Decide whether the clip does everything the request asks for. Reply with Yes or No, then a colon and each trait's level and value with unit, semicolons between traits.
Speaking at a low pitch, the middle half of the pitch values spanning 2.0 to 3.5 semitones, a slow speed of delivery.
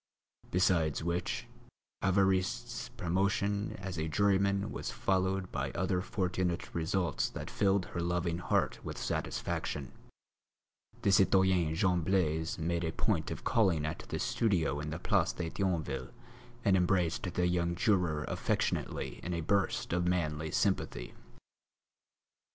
Yes: very low, 90 Hz; narrow, 2.6 semitones; slow, 130 wpm